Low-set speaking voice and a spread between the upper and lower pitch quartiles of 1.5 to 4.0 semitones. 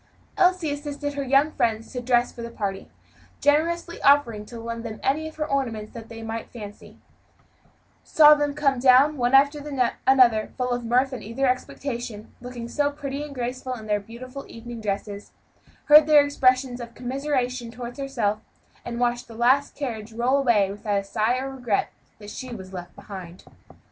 No: high, 245 Hz; average, 3.6 semitones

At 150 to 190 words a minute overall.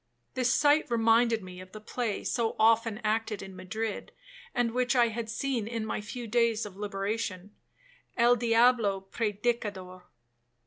No: average, 140 wpm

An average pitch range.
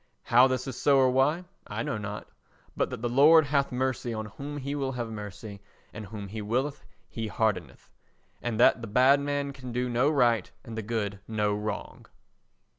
Yes: average, 3.9 semitones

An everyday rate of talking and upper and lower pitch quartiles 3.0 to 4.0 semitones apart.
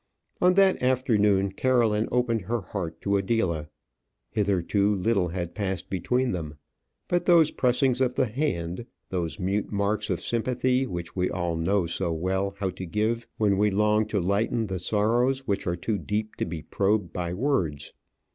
No: average, 165 wpm; average, 4.5 semitones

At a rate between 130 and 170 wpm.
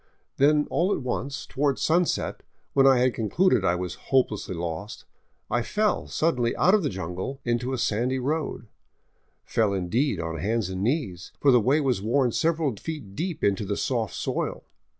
No: average, 180 wpm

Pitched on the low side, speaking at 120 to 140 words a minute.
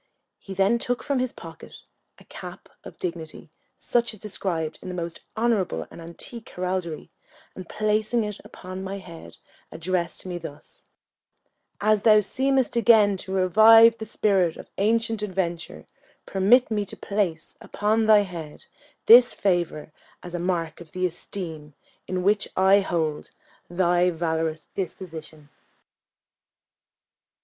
No: high, 190 Hz; slow, 135 wpm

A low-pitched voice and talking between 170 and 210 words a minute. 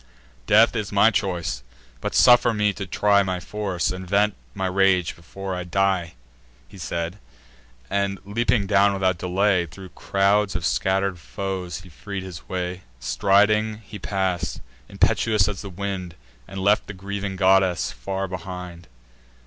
No: very low, 95 Hz; average, 150 wpm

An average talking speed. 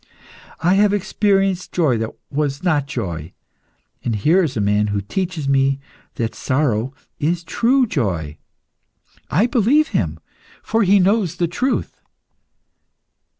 No: slow, 130 wpm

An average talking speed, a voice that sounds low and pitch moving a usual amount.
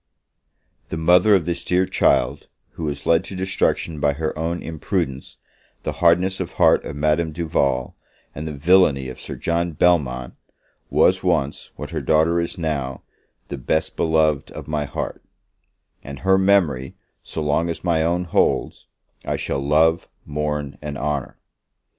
Yes: average, 155 wpm; very low, 80 Hz; average, 3.1 semitones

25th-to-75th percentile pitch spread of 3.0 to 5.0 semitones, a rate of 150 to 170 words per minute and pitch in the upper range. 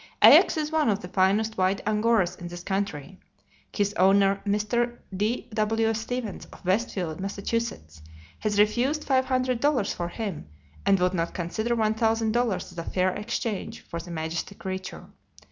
Yes: average, 3.7 semitones; average, 160 wpm; high, 205 Hz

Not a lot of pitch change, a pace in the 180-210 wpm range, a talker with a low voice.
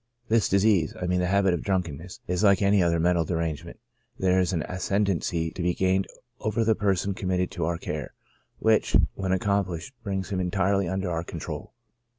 Yes: narrow, 2.2 semitones; average, 185 wpm; very low, 95 Hz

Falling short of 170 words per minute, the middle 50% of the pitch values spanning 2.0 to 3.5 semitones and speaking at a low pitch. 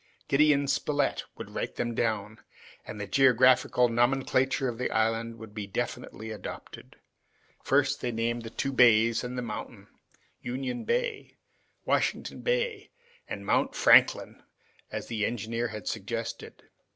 Yes: slow, 135 wpm; average, 3.2 semitones; low, 120 Hz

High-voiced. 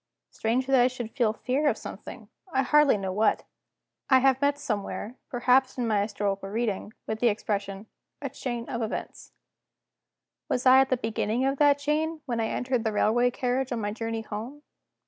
Yes: high, 245 Hz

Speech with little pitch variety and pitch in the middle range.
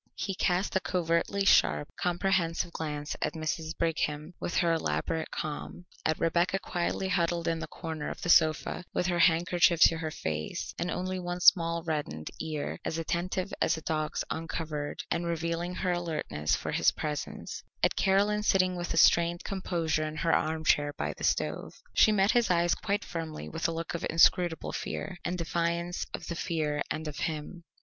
Yes: narrow, 2.0 semitones; medium, 170 Hz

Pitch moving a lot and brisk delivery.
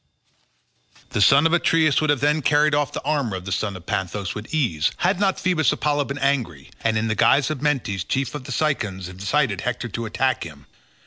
Yes: wide, 6.7 semitones; fast, 210 wpm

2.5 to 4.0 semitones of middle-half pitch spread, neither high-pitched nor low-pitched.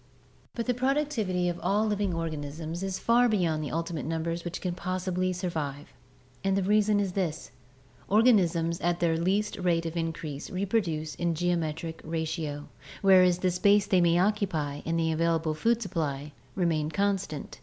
Yes: average, 3.2 semitones; medium, 175 Hz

